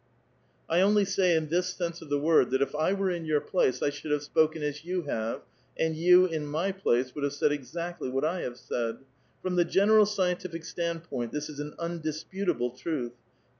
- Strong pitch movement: No, average, 3.6 semitones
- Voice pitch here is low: No, medium, 160 Hz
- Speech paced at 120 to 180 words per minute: No, fast, 205 wpm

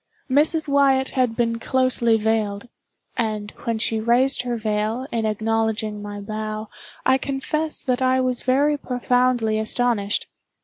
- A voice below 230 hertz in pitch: No, high, 235 Hz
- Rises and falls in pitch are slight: No, average, 3.1 semitones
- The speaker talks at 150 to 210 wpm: No, slow, 135 wpm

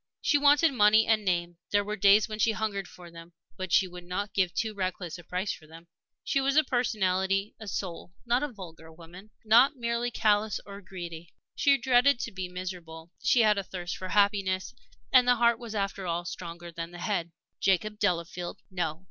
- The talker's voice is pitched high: Yes, high, 195 Hz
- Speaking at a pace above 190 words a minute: Yes, average, 200 wpm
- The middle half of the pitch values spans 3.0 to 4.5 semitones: Yes, average, 3.9 semitones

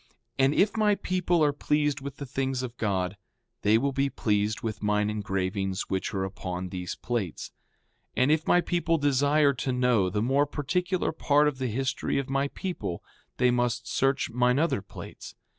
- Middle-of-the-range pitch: No, low, 130 Hz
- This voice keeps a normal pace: Yes, average, 180 wpm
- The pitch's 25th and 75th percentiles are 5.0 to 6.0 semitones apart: Yes, wide, 5.6 semitones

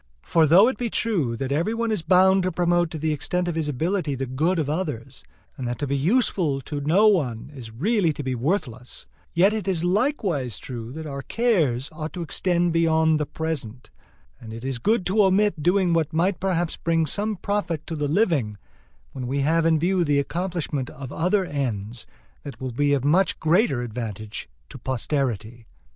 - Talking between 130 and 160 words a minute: No, average, 195 wpm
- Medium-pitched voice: Yes, medium, 160 Hz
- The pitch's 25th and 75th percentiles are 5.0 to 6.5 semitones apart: Yes, wide, 5.4 semitones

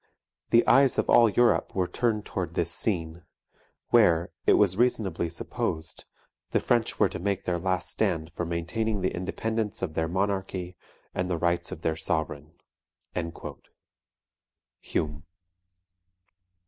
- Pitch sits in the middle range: No, very low, 90 Hz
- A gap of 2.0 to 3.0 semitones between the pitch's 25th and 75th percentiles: No, average, 3.6 semitones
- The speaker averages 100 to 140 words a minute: Yes, slow, 135 wpm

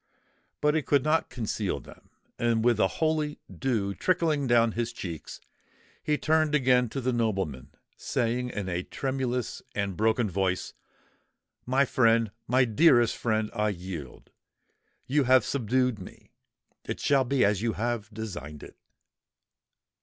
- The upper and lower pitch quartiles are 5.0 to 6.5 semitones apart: No, average, 4.2 semitones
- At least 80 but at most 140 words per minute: Yes, slow, 135 wpm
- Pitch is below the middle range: Yes, low, 120 Hz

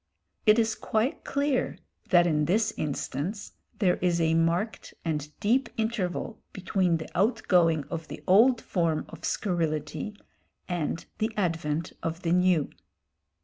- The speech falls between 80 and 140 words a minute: Yes, slow, 135 wpm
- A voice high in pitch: No, medium, 180 Hz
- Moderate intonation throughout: Yes, average, 4.7 semitones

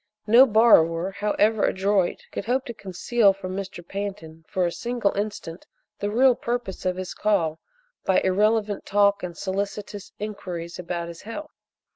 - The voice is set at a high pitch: Yes, high, 200 Hz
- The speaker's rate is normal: Yes, average, 150 wpm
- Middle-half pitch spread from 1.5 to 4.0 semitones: Yes, average, 2.8 semitones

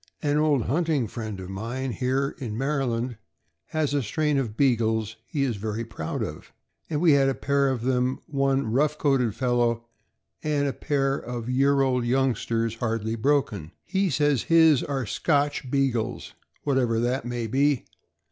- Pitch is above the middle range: No, low, 130 Hz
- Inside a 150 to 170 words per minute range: Yes, average, 165 wpm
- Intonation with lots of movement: No, average, 3.5 semitones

